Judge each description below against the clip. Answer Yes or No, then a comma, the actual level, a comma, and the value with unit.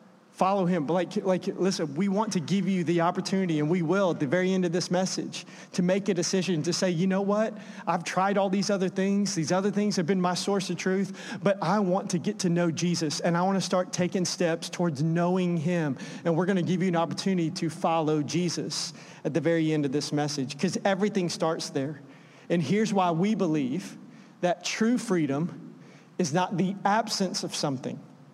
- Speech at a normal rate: No, fast, 215 wpm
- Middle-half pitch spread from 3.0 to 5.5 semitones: No, narrow, 2.5 semitones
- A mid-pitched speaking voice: Yes, medium, 180 Hz